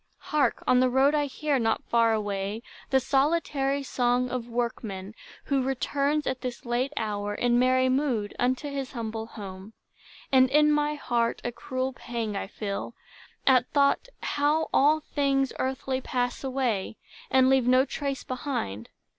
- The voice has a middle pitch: No, very high, 255 Hz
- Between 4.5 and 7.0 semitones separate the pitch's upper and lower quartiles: No, average, 3.0 semitones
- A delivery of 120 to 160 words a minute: Yes, average, 155 wpm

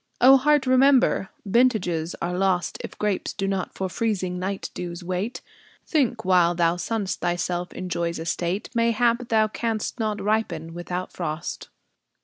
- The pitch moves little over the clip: No, average, 4.5 semitones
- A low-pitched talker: No, high, 190 Hz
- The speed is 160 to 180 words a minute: No, average, 145 wpm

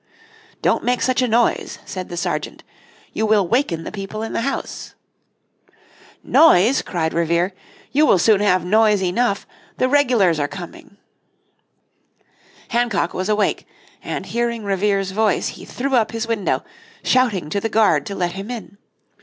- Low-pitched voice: No, high, 210 Hz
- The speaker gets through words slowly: No, average, 155 wpm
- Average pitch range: Yes, average, 4.2 semitones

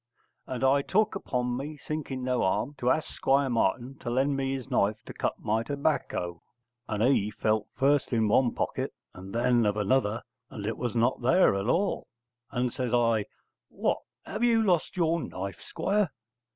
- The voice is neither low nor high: No, low, 125 Hz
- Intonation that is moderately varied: Yes, average, 4.3 semitones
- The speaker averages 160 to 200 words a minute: Yes, average, 180 wpm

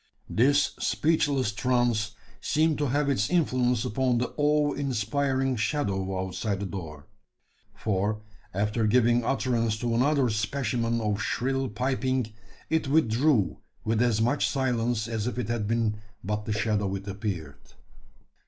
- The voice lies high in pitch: No, low, 120 Hz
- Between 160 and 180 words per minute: No, slow, 135 wpm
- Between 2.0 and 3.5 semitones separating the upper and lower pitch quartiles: No, average, 4.0 semitones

